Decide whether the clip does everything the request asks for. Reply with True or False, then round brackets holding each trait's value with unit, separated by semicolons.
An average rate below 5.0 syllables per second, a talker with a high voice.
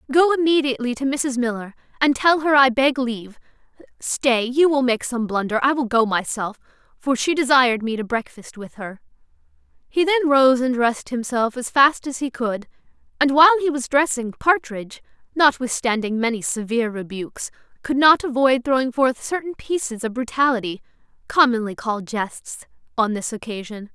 False (5.3 syllables/s; 250 Hz)